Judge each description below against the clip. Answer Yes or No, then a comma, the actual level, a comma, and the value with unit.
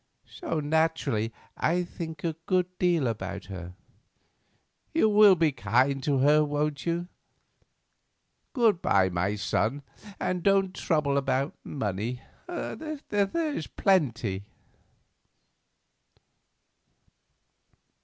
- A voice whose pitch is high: No, medium, 150 Hz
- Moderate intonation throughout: No, wide, 7.4 semitones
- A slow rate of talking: Yes, slow, 95 wpm